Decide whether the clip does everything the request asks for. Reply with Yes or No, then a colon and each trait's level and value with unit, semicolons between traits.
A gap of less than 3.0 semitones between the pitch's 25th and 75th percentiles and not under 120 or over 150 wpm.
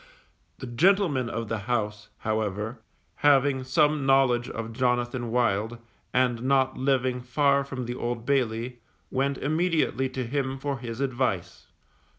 Yes: narrow, 2.6 semitones; slow, 135 wpm